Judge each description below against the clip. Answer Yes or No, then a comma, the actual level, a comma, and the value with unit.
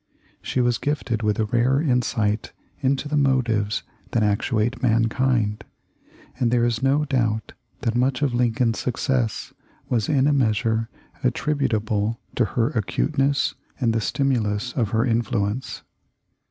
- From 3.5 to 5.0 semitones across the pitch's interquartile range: No, average, 3.0 semitones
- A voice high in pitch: No, low, 120 Hz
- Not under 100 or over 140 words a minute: Yes, slow, 135 wpm